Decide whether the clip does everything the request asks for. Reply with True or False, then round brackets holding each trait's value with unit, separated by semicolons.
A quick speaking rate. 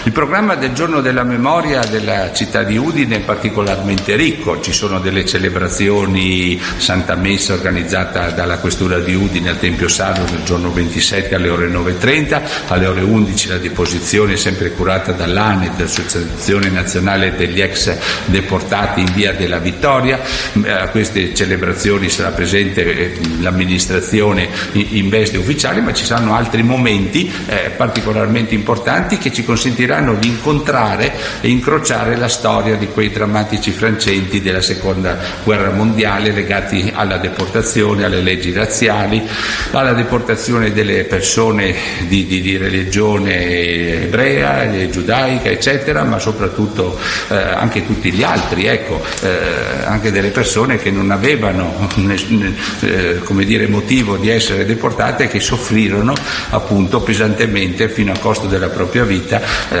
False (135 wpm)